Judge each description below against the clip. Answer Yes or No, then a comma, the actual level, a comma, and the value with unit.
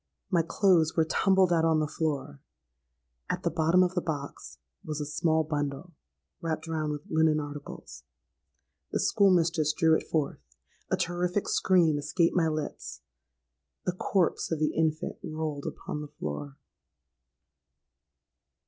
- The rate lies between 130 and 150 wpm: Yes, slow, 135 wpm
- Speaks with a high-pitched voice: No, medium, 155 Hz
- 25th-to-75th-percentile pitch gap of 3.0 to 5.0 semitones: No, narrow, 2.4 semitones